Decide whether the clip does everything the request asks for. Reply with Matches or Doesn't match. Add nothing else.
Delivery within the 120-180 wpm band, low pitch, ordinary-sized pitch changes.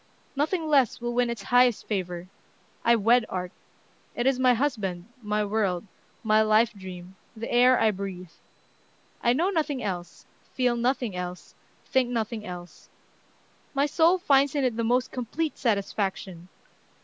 Doesn't match